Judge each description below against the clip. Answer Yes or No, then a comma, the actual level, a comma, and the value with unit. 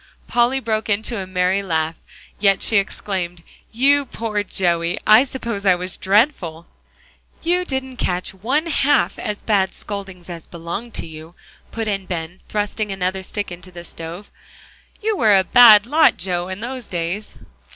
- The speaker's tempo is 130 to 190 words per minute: Yes, average, 160 wpm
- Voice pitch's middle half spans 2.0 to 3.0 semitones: No, average, 4.5 semitones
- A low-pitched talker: No, high, 200 Hz